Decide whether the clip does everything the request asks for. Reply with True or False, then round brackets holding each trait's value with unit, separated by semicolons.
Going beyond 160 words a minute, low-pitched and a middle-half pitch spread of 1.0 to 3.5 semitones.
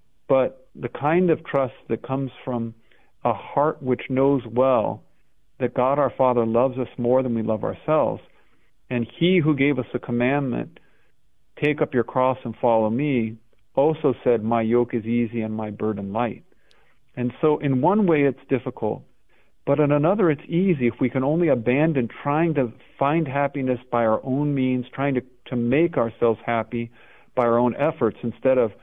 True (175 wpm; 130 Hz; 3.1 semitones)